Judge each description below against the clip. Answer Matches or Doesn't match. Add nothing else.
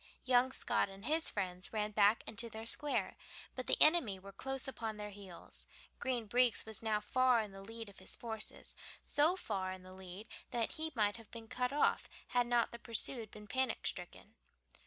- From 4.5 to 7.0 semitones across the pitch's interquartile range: Doesn't match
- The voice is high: Matches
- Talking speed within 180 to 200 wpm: Matches